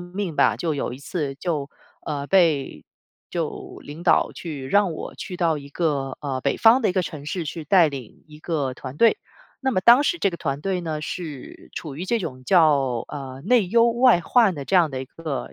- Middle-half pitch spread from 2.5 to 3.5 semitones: No, average, 4.8 semitones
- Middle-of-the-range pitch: Yes, medium, 160 Hz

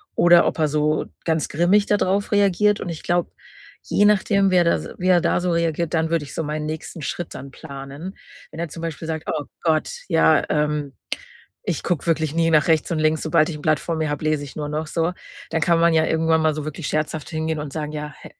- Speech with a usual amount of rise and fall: No, narrow, 1.9 semitones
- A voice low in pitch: No, medium, 160 Hz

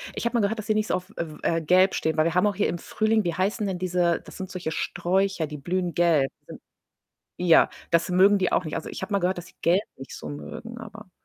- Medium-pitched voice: Yes, medium, 180 Hz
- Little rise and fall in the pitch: No, average, 3.0 semitones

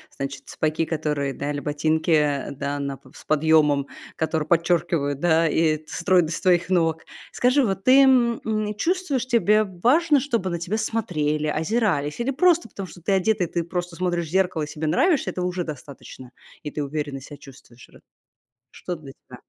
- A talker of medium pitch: Yes, medium, 170 Hz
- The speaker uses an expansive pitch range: Yes, wide, 5.8 semitones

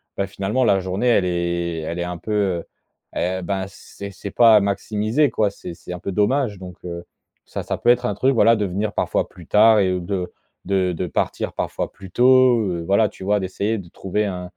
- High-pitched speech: No, low, 100 Hz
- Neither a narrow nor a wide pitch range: Yes, average, 3.1 semitones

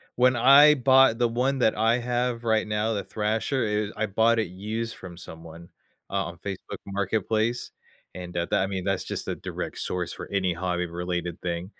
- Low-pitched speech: Yes, low, 105 Hz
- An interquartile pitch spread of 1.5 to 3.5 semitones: No, average, 4.4 semitones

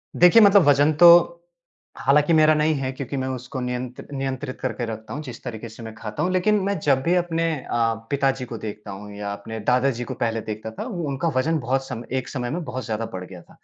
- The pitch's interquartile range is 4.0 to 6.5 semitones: Yes, average, 5.0 semitones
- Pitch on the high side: No, low, 130 Hz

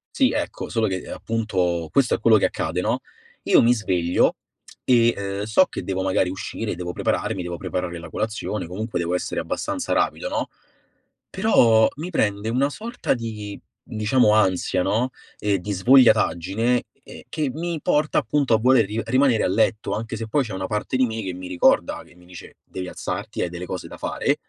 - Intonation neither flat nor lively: Yes, average, 4.8 semitones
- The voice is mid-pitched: No, low, 110 Hz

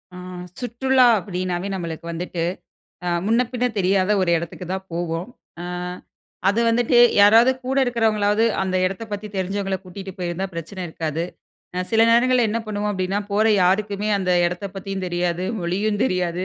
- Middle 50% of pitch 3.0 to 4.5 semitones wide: Yes, average, 3.3 semitones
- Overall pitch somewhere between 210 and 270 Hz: No, high, 195 Hz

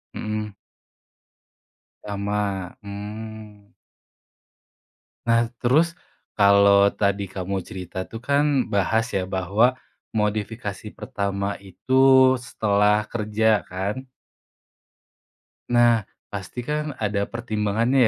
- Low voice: Yes, low, 105 Hz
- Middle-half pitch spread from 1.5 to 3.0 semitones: Yes, narrow, 2.4 semitones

